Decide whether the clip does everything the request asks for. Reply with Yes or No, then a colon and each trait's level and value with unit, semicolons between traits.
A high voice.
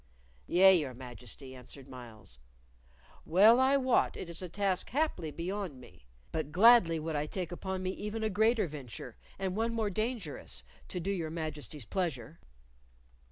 No: medium, 175 Hz